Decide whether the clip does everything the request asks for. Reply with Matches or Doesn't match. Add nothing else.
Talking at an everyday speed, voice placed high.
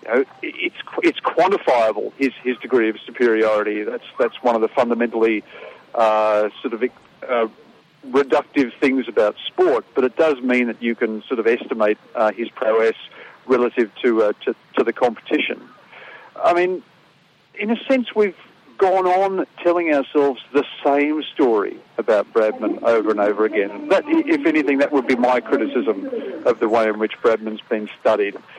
Doesn't match